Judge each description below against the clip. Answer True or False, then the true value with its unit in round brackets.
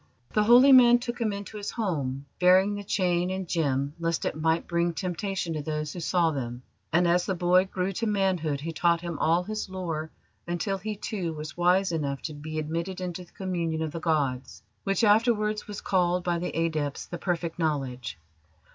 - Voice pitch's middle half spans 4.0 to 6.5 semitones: False (3.5 semitones)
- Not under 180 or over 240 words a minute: True (195 wpm)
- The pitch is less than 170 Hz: False (175 Hz)